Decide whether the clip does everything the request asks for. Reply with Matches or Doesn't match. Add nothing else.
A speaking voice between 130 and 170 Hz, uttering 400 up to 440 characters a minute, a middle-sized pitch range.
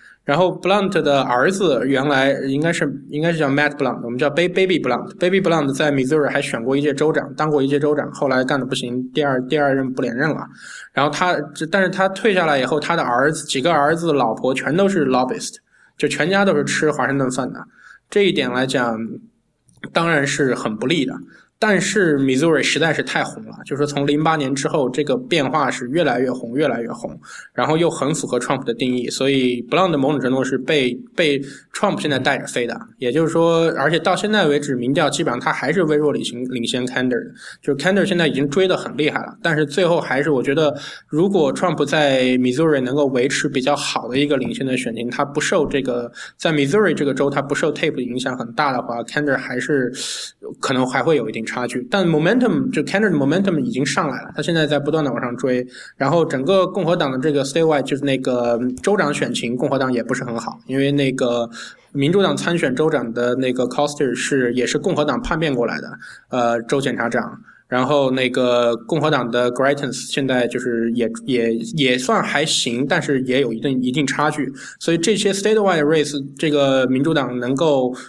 Matches